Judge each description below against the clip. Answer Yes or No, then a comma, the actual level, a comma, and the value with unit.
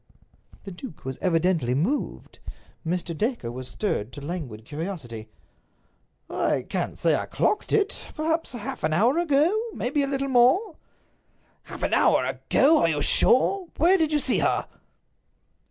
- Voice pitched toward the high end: Yes, high, 210 Hz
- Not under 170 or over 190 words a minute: No, average, 150 wpm